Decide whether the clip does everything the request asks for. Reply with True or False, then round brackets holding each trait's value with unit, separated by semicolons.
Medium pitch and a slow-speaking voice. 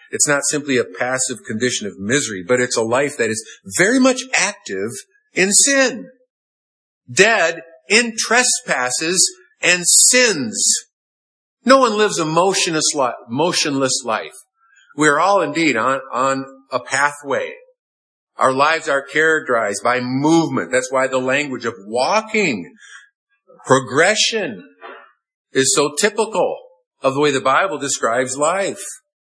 True (160 Hz; 125 wpm)